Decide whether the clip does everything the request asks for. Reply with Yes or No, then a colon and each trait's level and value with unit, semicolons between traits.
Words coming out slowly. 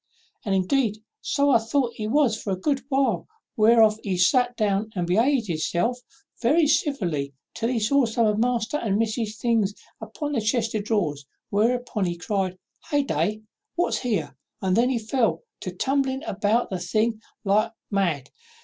No: average, 170 wpm